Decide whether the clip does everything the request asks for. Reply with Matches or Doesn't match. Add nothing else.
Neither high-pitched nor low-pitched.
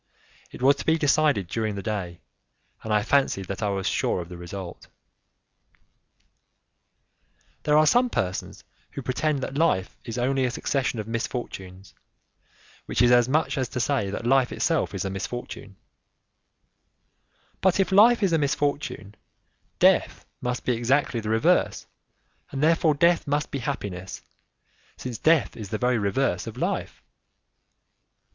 Doesn't match